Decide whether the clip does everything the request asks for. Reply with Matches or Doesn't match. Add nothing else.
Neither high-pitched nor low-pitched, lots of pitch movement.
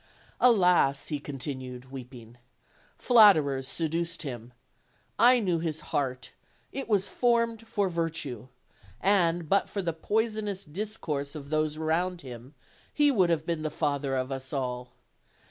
Matches